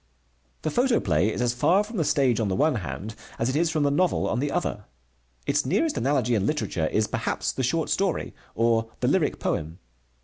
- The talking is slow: No, fast, 205 wpm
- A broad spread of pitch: Yes, wide, 6.1 semitones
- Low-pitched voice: Yes, low, 130 Hz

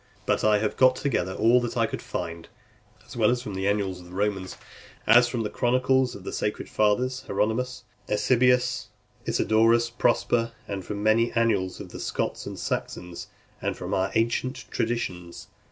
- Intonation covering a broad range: No, average, 3.4 semitones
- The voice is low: Yes, low, 110 Hz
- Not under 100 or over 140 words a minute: No, average, 170 wpm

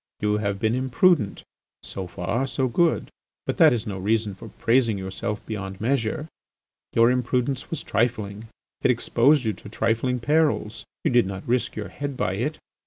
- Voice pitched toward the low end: Yes, low, 115 Hz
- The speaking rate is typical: Yes, average, 170 wpm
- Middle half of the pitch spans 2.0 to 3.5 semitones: No, average, 4.0 semitones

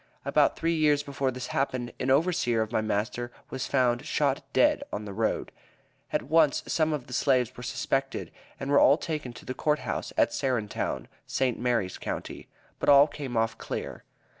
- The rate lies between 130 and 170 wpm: No, average, 185 wpm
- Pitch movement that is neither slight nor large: Yes, average, 3.0 semitones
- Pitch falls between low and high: No, low, 130 Hz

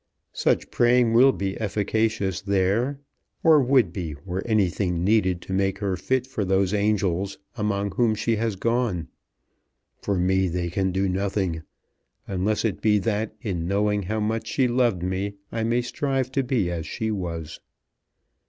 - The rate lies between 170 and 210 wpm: No, average, 160 wpm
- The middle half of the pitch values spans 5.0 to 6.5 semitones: No, average, 3.3 semitones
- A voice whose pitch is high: No, low, 100 Hz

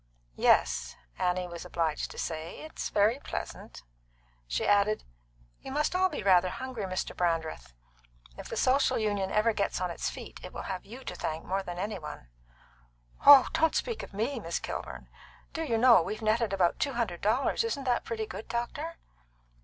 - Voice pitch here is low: No, high, 205 Hz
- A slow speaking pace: No, average, 180 wpm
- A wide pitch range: Yes, wide, 6.2 semitones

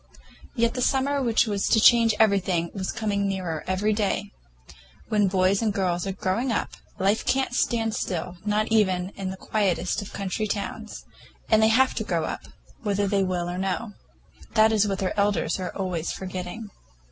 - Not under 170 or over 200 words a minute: Yes, average, 180 wpm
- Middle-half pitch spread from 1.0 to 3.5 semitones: Yes, average, 2.8 semitones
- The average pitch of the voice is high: Yes, high, 200 Hz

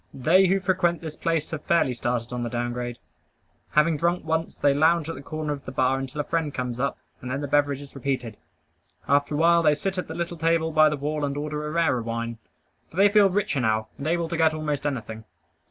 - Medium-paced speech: No, fast, 235 wpm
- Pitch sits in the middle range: Yes, medium, 150 Hz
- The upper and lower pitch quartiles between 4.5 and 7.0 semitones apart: No, average, 4.1 semitones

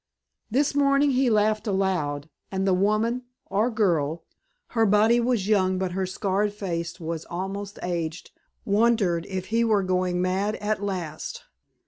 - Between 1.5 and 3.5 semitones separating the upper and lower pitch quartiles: Yes, average, 3.0 semitones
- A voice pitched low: No, high, 195 Hz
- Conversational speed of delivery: Yes, average, 145 wpm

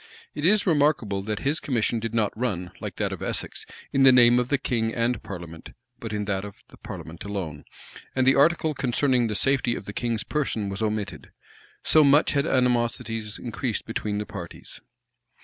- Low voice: Yes, low, 115 Hz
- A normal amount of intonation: Yes, average, 4.5 semitones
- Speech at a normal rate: Yes, average, 190 wpm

